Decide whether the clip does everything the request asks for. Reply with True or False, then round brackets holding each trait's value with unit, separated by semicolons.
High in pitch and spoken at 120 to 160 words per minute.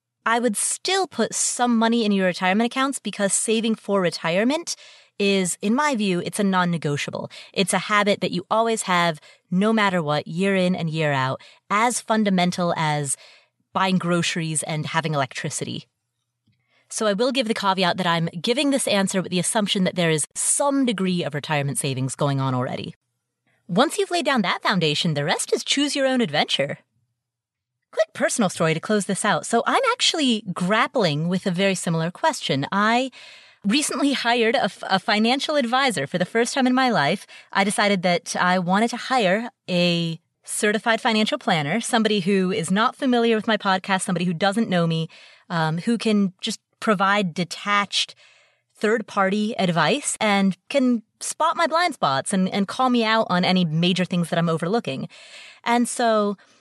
False (200 Hz; 175 wpm)